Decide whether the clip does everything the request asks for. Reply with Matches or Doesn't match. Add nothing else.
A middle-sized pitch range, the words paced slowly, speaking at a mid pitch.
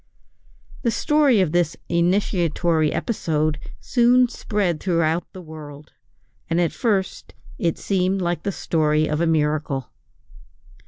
Matches